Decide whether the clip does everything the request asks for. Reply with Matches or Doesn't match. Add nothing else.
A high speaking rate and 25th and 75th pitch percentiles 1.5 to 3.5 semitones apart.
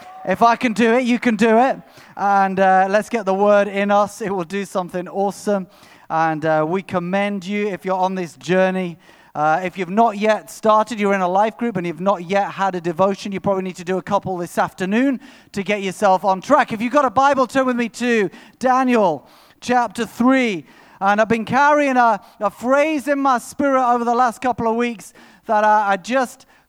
Doesn't match